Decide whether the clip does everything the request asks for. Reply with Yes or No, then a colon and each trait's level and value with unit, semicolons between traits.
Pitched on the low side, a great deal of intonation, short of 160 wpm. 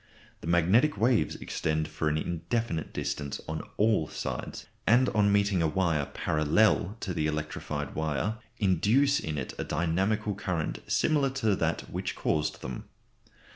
Yes: very low, 85 Hz; wide, 5.7 semitones; average, 145 wpm